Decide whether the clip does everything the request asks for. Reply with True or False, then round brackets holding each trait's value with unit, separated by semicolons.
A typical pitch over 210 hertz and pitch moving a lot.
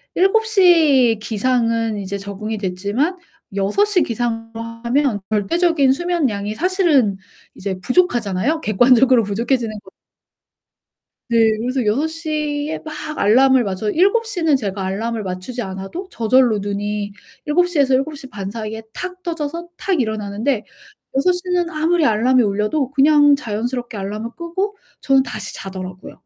True (245 Hz; 6.8 semitones)